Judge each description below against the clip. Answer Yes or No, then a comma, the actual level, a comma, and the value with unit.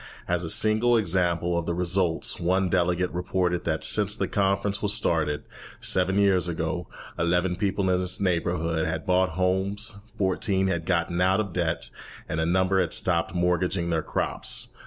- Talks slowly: No, average, 165 wpm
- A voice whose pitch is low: Yes, very low, 90 Hz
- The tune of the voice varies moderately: No, narrow, 2.0 semitones